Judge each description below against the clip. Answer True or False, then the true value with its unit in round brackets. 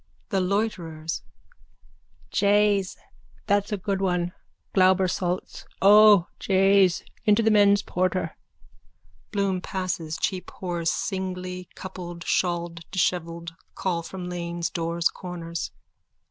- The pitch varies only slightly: True (2.3 semitones)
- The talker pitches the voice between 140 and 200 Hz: True (185 Hz)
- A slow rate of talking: True (105 wpm)